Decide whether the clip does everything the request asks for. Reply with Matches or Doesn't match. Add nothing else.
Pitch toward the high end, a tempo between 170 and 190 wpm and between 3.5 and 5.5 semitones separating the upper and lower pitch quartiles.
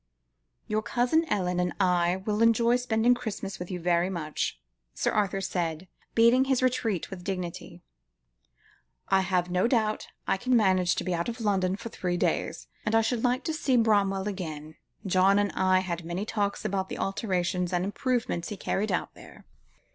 Matches